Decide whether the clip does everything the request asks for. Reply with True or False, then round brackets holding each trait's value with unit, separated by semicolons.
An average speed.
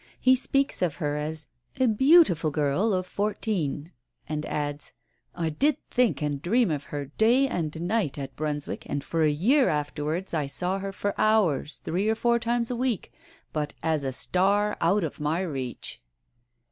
True (170 wpm)